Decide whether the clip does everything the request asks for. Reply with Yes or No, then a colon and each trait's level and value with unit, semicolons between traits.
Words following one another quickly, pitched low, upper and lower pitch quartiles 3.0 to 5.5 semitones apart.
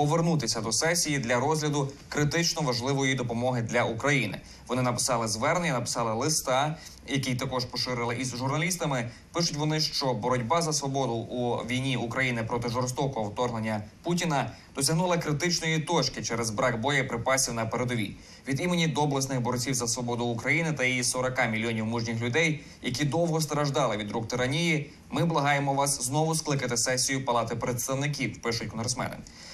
No: average, 140 wpm; low, 130 Hz; average, 3.7 semitones